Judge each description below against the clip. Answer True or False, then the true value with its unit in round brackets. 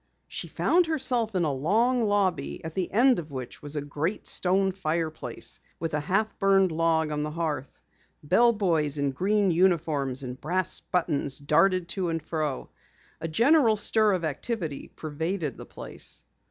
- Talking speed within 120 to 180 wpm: True (160 wpm)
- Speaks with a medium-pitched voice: True (170 Hz)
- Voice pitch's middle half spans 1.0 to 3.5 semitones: False (4.9 semitones)